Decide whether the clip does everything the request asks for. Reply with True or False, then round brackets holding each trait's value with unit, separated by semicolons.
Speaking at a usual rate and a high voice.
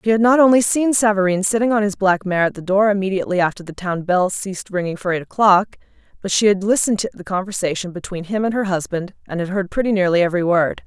False (235 wpm; 195 Hz)